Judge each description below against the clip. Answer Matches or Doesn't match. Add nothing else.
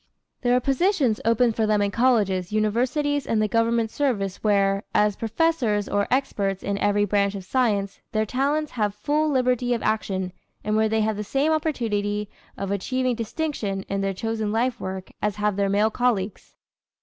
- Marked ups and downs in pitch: Doesn't match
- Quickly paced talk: Doesn't match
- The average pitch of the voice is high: Matches